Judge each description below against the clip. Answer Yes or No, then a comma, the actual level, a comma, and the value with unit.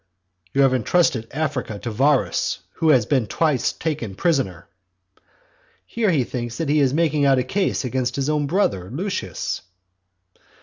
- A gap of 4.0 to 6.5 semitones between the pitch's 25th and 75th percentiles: Yes, average, 4.5 semitones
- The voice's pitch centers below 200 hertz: Yes, low, 135 Hz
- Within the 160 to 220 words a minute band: No, average, 150 wpm